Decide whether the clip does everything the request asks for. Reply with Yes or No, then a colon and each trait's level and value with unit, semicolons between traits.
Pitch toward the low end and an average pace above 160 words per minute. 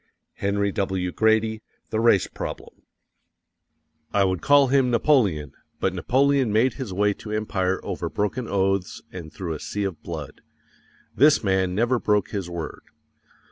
No: low, 100 Hz; average, 150 wpm